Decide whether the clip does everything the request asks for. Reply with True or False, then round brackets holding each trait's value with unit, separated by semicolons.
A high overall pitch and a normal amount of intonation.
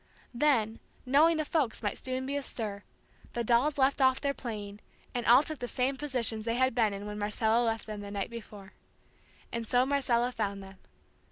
True (235 Hz; 3.8 semitones)